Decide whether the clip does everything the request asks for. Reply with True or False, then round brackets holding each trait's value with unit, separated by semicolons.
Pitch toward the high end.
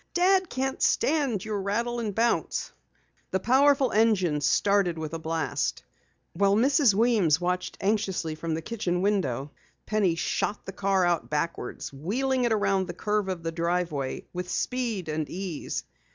True (195 Hz)